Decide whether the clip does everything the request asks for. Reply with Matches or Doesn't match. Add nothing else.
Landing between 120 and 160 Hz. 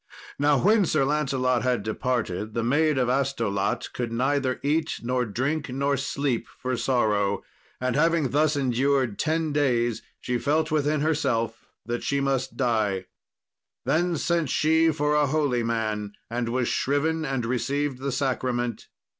Matches